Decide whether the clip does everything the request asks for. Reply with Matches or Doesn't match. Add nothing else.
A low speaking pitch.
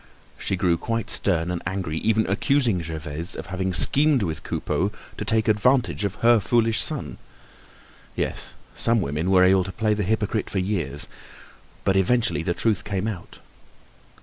Matches